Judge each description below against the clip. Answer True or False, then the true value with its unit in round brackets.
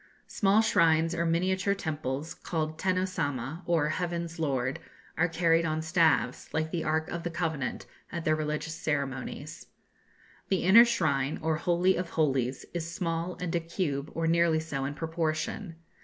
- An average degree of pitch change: False (2.0 semitones)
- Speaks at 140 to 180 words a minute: True (155 wpm)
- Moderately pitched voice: True (165 Hz)